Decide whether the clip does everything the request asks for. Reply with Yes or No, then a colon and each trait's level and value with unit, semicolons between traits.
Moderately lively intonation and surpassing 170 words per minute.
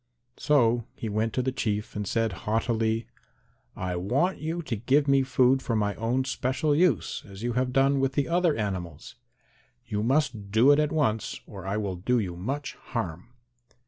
Yes: average, 4.6 semitones; average, 180 wpm